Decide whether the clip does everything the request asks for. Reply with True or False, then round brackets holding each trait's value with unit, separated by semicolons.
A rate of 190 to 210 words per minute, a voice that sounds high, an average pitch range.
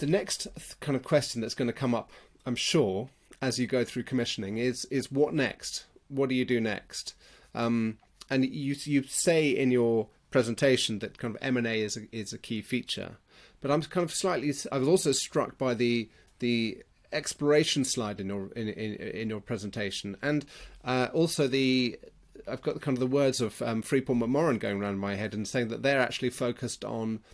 False (200 wpm; 125 Hz; 3.4 semitones)